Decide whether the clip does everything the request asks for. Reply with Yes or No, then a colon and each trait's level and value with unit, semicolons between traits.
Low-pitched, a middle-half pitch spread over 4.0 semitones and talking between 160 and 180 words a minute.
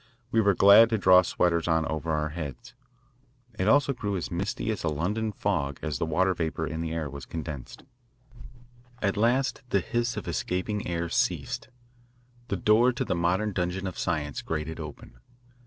Yes: very low, 90 Hz; average, 4.5 semitones; average, 175 wpm